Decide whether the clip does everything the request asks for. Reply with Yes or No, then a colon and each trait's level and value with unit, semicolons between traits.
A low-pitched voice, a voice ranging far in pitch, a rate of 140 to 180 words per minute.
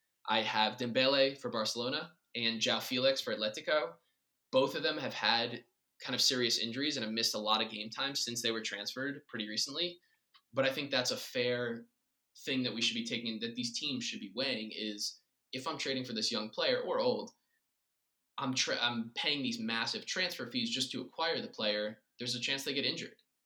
No: low, 130 Hz; wide, 7.5 semitones; fast, 205 wpm